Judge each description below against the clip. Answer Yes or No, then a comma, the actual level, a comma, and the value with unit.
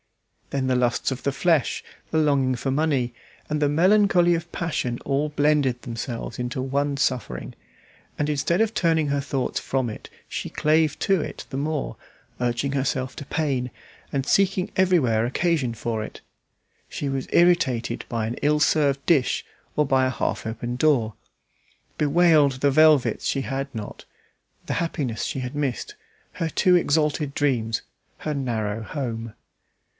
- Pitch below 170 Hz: Yes, medium, 140 Hz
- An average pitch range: Yes, average, 3.7 semitones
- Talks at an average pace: Yes, average, 155 wpm